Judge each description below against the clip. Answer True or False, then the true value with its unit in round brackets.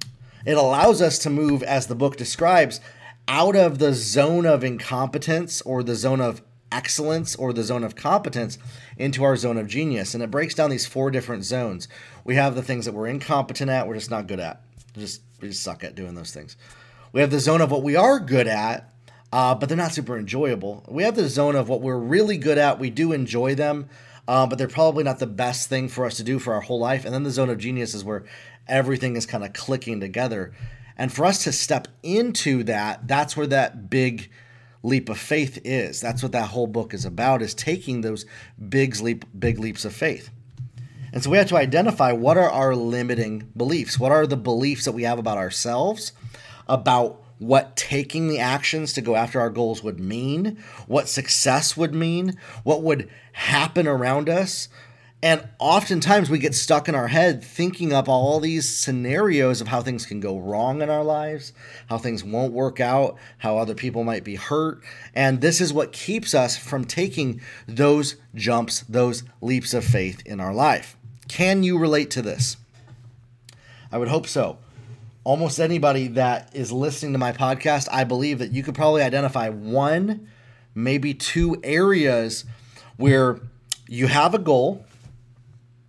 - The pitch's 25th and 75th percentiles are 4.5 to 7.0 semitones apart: False (3.5 semitones)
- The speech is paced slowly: False (190 wpm)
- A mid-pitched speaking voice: False (130 Hz)